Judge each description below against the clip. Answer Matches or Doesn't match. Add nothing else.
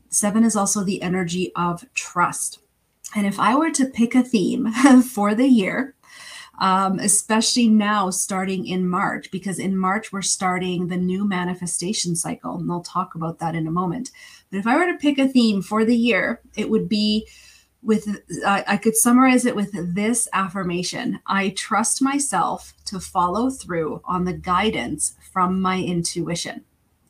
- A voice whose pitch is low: Doesn't match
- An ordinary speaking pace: Matches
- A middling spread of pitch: Matches